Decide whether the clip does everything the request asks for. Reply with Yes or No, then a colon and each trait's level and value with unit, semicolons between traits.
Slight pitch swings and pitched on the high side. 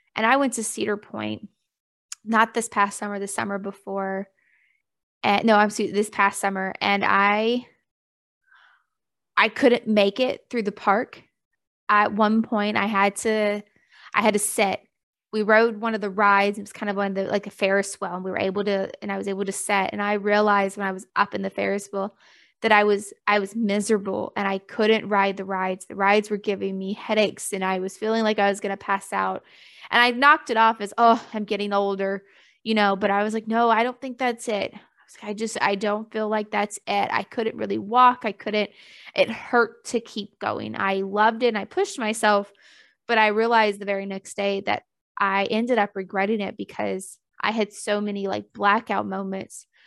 Yes: narrow, 1.8 semitones; high, 205 Hz